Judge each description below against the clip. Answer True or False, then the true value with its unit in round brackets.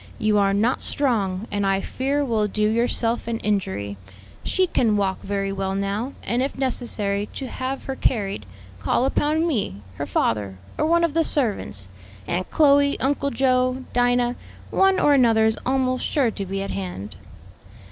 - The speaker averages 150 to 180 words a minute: True (165 wpm)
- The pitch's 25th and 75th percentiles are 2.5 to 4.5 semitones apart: False (5.2 semitones)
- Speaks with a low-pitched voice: False (230 Hz)